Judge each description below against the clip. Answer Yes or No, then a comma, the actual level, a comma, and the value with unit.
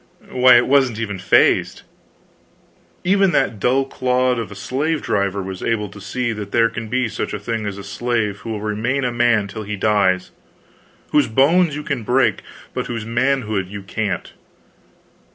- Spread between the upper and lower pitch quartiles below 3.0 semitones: No, average, 3.8 semitones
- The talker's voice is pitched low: Yes, low, 115 Hz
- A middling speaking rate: Yes, average, 175 wpm